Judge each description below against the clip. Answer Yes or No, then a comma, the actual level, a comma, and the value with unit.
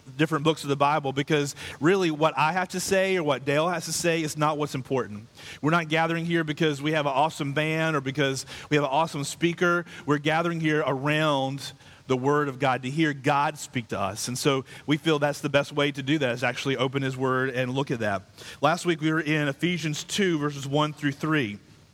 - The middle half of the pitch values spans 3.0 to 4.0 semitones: No, narrow, 2.6 semitones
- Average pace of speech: No, fast, 230 wpm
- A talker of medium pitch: Yes, medium, 150 Hz